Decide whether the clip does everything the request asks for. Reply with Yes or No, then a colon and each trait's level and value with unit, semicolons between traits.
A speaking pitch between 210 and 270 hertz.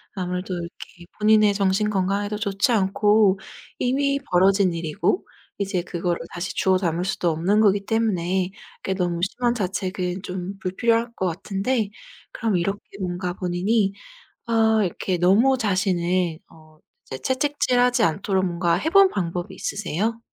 No: high, 195 Hz